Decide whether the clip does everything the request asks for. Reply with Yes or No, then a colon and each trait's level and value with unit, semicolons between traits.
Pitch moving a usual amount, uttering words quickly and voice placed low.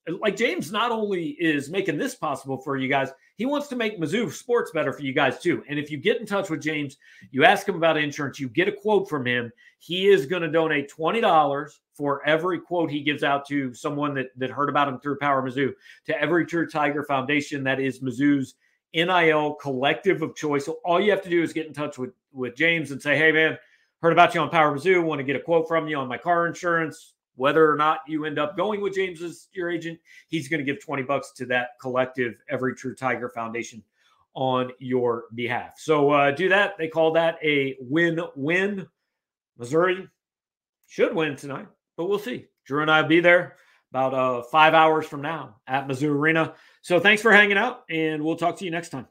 No: average, 3.6 semitones; fast, 220 wpm; medium, 155 Hz